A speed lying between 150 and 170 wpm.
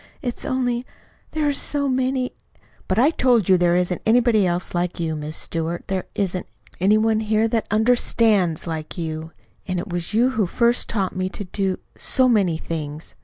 No: average, 180 wpm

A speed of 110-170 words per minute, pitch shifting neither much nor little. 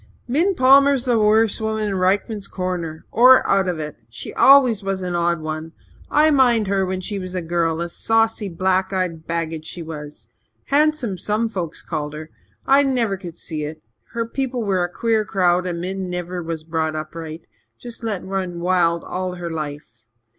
No: average, 185 wpm; average, 5.0 semitones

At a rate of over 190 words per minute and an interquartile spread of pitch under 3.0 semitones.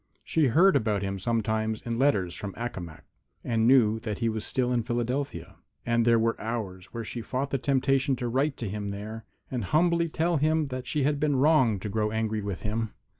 No: fast, 205 wpm; average, 4.0 semitones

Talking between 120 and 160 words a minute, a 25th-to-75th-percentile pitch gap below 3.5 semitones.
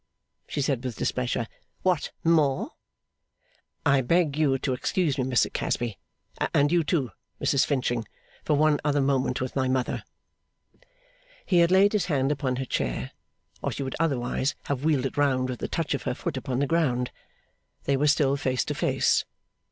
No: average, 175 wpm; average, 2.9 semitones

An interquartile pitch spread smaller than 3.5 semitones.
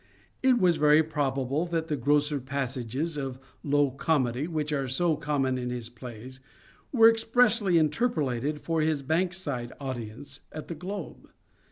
No: average, 4.0 semitones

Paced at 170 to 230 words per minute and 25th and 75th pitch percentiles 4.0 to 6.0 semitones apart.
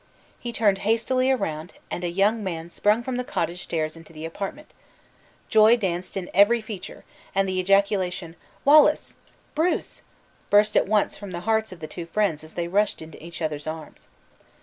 Yes: average, 175 wpm; average, 4.4 semitones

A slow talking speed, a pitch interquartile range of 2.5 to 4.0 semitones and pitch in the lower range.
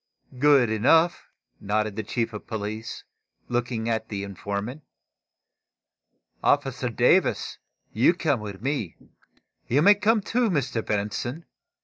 No: slow, 115 wpm; wide, 5.6 semitones; low, 115 Hz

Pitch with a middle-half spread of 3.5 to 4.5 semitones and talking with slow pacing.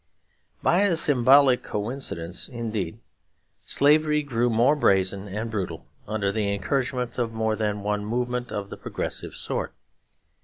Yes: average, 4.1 semitones; slow, 130 wpm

